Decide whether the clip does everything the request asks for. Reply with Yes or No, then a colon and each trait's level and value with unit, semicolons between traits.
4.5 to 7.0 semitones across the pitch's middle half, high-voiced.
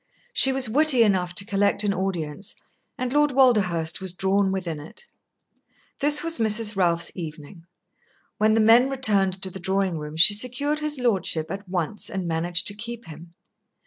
Yes: average, 5.3 semitones; high, 195 Hz